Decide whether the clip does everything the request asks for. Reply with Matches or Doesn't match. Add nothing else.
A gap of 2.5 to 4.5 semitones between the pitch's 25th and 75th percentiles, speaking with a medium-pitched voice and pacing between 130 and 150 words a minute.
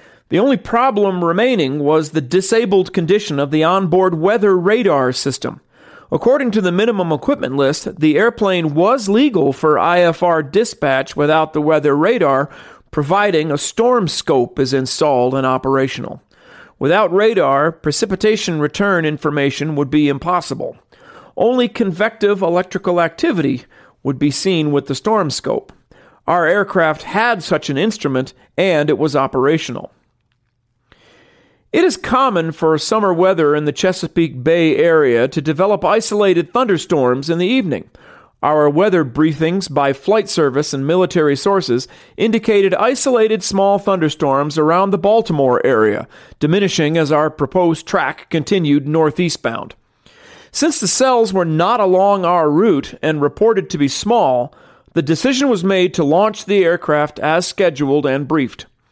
Doesn't match